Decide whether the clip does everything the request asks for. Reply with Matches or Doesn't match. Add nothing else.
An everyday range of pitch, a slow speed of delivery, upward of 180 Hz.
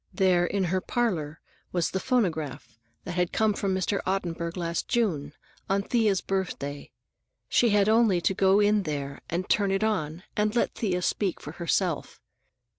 Doesn't match